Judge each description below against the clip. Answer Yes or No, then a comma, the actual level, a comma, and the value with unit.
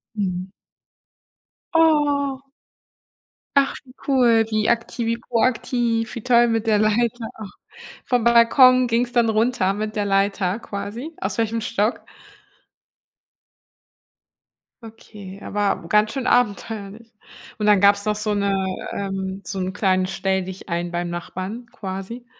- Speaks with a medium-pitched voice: No, high, 215 Hz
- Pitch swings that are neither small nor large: Yes, average, 3.3 semitones